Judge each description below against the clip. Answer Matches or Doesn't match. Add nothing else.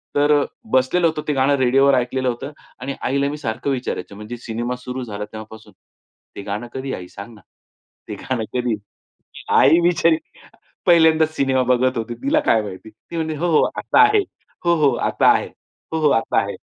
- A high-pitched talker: Doesn't match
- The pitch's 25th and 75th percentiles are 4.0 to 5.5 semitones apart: Matches